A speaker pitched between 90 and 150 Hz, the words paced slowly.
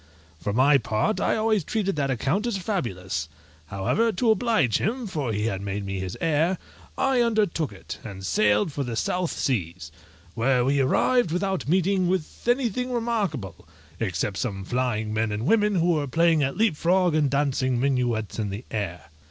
No: medium, 140 Hz; average, 175 wpm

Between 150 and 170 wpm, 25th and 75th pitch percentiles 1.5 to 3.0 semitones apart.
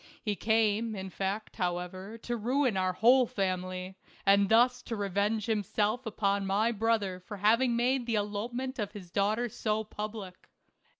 Yes: average, 155 wpm; average, 2.7 semitones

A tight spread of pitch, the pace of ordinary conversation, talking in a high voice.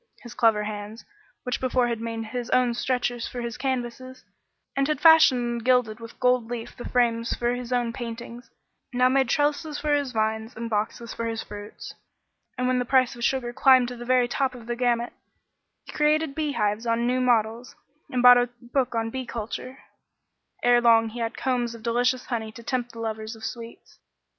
Yes: narrow, 1.8 semitones; average, 195 wpm; high, 240 Hz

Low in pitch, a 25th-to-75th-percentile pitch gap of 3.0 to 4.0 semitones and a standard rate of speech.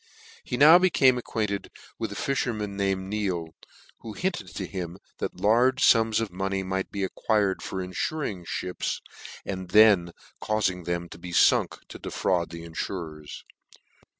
Yes: low, 100 Hz; average, 3.7 semitones; average, 150 wpm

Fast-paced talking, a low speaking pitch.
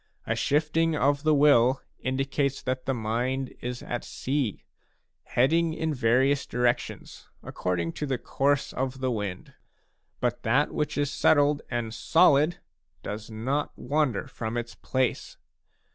No: average, 140 wpm; low, 130 Hz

